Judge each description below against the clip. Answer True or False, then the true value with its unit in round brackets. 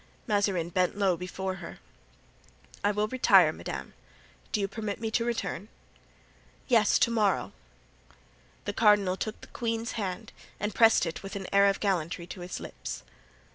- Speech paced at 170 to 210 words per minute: False (155 wpm)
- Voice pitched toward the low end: False (200 Hz)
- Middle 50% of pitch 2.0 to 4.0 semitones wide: True (2.9 semitones)